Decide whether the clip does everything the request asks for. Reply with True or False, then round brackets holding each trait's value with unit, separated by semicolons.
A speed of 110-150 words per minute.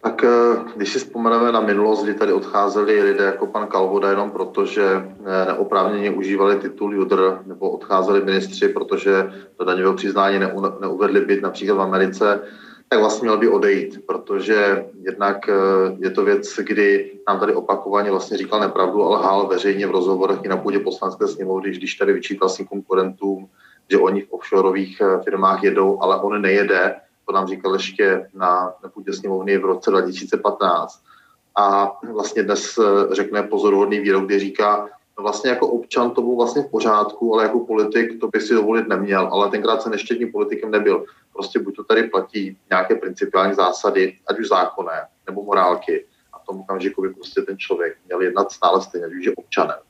False (170 wpm)